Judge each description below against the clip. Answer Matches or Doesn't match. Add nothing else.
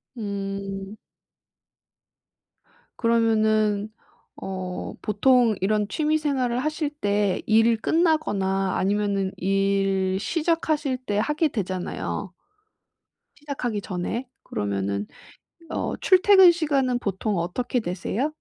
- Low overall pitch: Doesn't match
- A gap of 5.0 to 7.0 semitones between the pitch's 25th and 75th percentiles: Matches